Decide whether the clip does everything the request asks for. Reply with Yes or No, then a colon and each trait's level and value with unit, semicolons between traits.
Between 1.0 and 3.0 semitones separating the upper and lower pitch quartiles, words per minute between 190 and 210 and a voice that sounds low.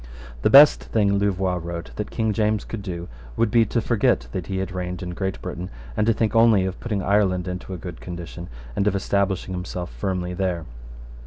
Yes: narrow, 2.6 semitones; average, 200 wpm; very low, 95 Hz